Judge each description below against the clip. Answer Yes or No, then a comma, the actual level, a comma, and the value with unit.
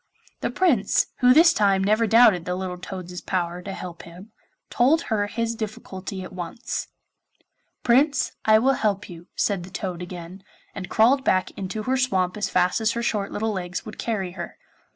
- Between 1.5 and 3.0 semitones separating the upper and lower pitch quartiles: No, average, 3.9 semitones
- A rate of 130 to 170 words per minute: No, average, 180 wpm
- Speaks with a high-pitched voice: Yes, high, 200 Hz